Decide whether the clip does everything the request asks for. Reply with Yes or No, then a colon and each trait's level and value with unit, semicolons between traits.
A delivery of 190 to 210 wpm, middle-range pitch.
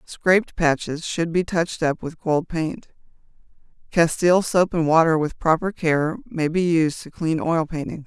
No: average, 170 wpm; medium, 165 Hz